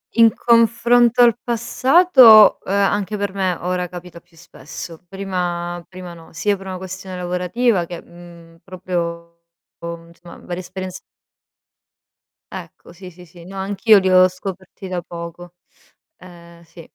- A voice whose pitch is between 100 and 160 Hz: No, medium, 185 Hz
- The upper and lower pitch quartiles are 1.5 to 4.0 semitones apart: Yes, narrow, 2.5 semitones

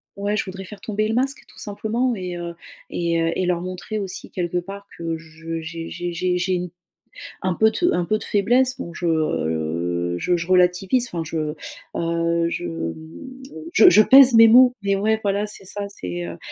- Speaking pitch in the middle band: Yes, medium, 180 Hz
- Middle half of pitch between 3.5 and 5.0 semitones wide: Yes, average, 4.3 semitones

